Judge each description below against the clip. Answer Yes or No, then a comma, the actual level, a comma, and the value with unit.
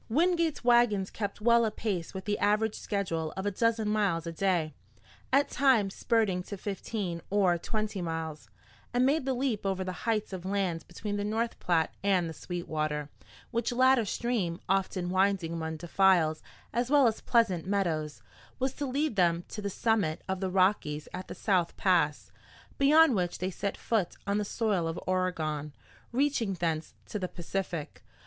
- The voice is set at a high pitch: Yes, high, 195 Hz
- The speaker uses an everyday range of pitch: Yes, average, 4.6 semitones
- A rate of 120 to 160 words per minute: No, average, 170 wpm